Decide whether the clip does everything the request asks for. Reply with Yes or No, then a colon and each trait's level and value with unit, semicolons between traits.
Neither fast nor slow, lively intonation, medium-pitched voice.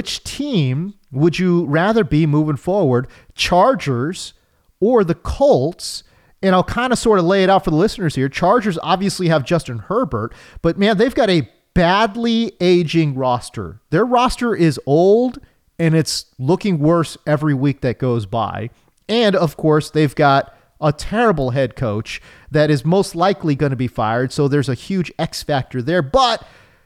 Yes: average, 170 wpm; wide, 6.0 semitones; medium, 160 Hz